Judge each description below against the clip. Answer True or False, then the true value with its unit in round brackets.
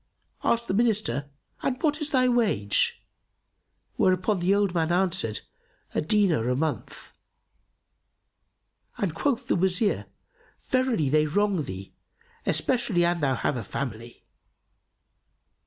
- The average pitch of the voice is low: False (185 Hz)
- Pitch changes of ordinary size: False (7.7 semitones)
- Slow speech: True (120 wpm)